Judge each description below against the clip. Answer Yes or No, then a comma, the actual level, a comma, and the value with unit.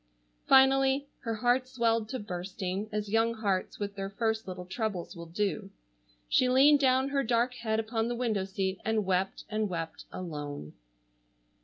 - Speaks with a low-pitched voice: No, high, 215 Hz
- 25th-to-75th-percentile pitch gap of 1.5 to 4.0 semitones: No, average, 4.4 semitones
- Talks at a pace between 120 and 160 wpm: Yes, average, 150 wpm